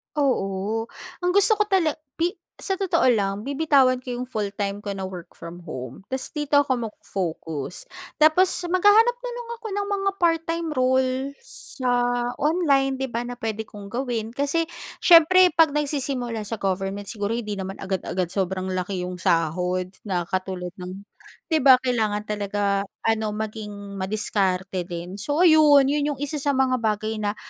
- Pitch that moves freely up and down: Yes, wide, 6.9 semitones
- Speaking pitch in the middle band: No, high, 225 Hz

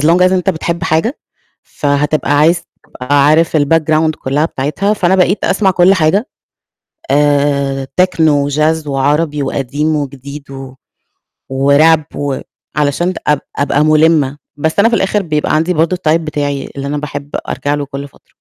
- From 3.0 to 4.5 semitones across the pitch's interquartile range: No, narrow, 2.5 semitones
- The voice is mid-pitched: Yes, medium, 150 Hz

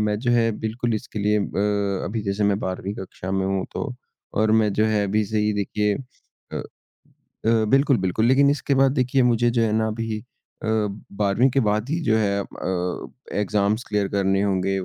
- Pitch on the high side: No, low, 105 Hz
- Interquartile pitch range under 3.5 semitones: Yes, narrow, 2.6 semitones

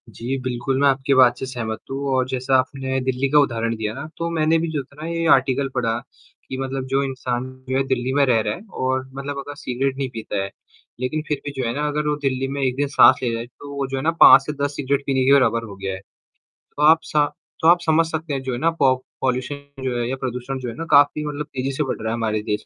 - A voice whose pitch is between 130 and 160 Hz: Yes, low, 135 Hz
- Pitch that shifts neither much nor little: No, narrow, 2.2 semitones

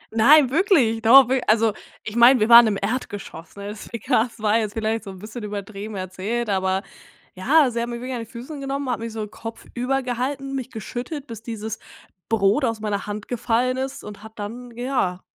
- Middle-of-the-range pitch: No, high, 230 Hz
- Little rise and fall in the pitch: No, average, 3.2 semitones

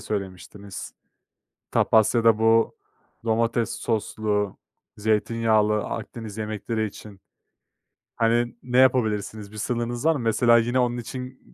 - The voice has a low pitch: Yes, low, 115 Hz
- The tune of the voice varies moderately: No, narrow, 1.9 semitones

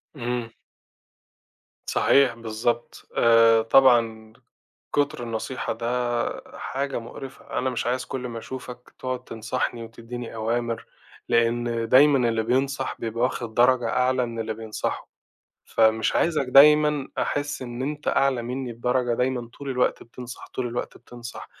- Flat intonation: Yes, narrow, 2.1 semitones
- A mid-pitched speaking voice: No, low, 120 Hz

